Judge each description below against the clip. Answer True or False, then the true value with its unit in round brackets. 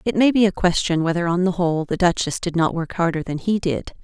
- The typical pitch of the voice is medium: True (180 Hz)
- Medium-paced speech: False (270 wpm)